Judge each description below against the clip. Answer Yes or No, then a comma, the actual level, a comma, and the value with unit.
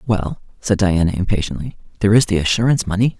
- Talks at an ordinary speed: Yes, average, 170 wpm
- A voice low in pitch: Yes, low, 100 Hz